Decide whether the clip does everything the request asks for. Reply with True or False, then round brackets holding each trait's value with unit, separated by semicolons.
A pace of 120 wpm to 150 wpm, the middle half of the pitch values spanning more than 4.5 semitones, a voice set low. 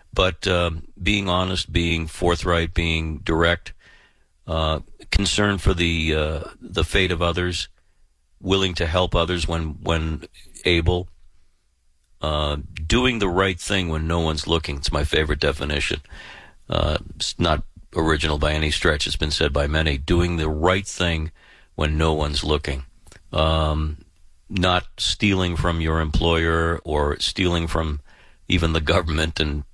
False (140 wpm; 2.4 semitones; 80 Hz)